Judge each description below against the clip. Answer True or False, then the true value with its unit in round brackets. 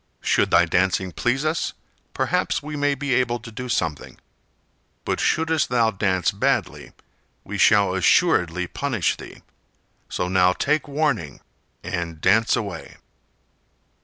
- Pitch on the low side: True (110 Hz)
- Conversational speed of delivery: False (130 wpm)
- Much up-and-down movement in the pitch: True (7.5 semitones)